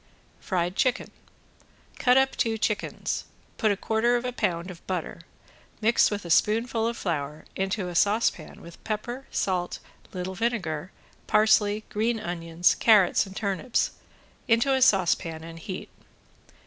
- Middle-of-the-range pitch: No, high, 205 Hz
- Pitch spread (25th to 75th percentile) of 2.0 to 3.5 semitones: No, average, 4.5 semitones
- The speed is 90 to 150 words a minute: Yes, average, 140 wpm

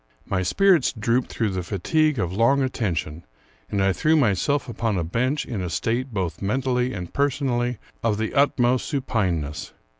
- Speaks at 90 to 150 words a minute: No, average, 160 wpm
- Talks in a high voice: No, low, 115 Hz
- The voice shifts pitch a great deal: Yes, wide, 5.9 semitones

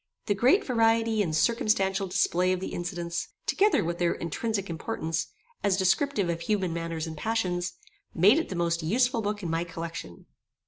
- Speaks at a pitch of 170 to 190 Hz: Yes, medium, 185 Hz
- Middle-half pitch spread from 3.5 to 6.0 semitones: Yes, average, 4.7 semitones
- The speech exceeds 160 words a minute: Yes, average, 170 wpm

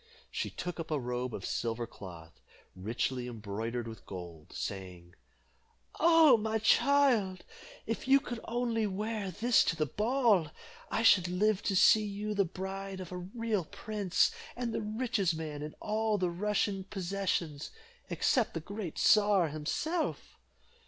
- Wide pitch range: Yes, wide, 6.6 semitones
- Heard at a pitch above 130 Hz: Yes, high, 190 Hz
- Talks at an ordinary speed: Yes, average, 145 wpm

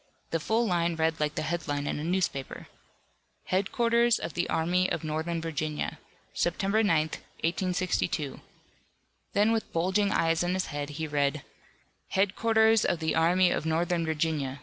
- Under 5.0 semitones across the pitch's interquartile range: Yes, average, 3.3 semitones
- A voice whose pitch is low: No, medium, 170 Hz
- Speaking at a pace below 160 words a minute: Yes, average, 150 wpm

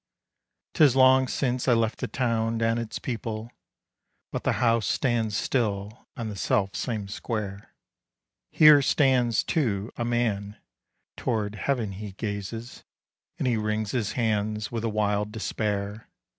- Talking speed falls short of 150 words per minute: Yes, average, 140 wpm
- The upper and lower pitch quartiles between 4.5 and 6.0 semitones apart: No, narrow, 2.5 semitones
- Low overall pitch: Yes, low, 110 Hz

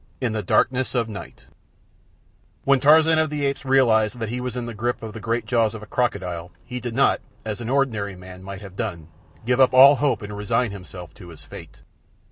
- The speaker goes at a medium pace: No, fast, 220 wpm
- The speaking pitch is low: Yes, low, 115 Hz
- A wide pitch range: No, average, 4.3 semitones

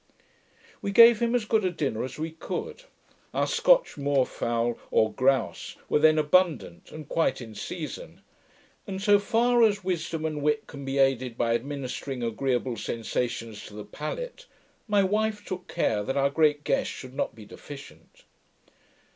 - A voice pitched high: No, medium, 150 Hz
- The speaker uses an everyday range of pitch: No, wide, 8.1 semitones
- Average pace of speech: Yes, average, 165 wpm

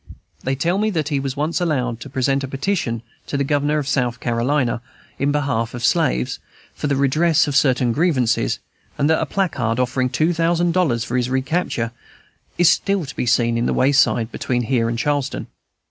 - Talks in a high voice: No, low, 135 Hz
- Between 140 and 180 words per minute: No, average, 190 wpm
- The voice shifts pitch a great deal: No, average, 4.0 semitones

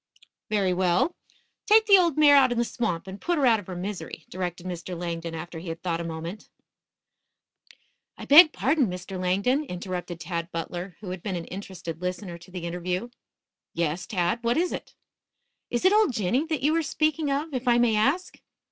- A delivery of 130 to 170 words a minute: No, average, 195 wpm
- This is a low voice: No, high, 190 Hz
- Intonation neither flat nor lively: No, wide, 7.3 semitones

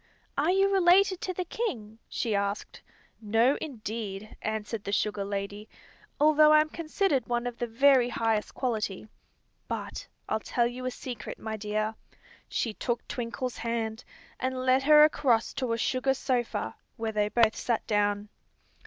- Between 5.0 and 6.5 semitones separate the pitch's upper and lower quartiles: No, average, 4.1 semitones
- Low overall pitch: No, high, 235 Hz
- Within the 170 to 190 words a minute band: No, average, 155 wpm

